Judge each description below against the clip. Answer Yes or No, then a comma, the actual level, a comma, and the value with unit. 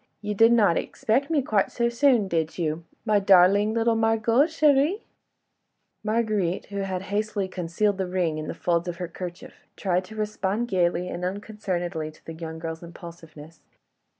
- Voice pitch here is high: Yes, high, 195 Hz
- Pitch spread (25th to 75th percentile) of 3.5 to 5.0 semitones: Yes, average, 4.2 semitones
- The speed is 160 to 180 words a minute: Yes, average, 165 wpm